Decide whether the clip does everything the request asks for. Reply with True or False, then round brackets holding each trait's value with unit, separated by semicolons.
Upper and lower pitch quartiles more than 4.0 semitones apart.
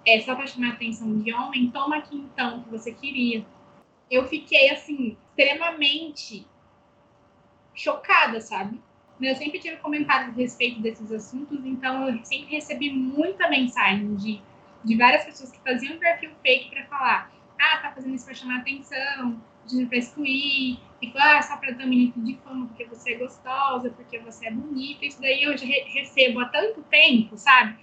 False (2.9 semitones)